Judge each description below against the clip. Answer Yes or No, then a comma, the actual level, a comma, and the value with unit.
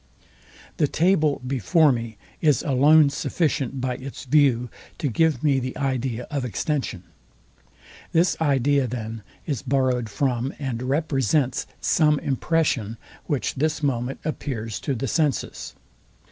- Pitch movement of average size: Yes, average, 3.3 semitones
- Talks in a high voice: No, low, 135 Hz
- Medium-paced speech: No, slow, 125 wpm